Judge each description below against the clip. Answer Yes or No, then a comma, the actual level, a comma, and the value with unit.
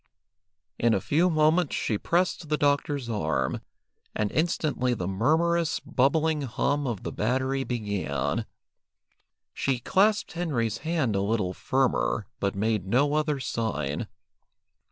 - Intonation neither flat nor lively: No, wide, 6.2 semitones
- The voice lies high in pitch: No, low, 130 Hz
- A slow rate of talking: Yes, slow, 125 wpm